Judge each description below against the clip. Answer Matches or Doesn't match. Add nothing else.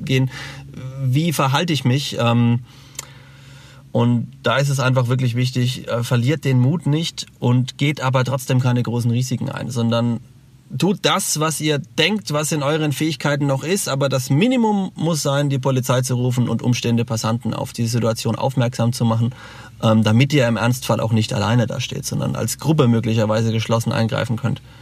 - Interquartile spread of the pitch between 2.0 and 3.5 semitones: Matches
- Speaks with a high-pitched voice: Doesn't match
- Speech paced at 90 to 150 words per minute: Doesn't match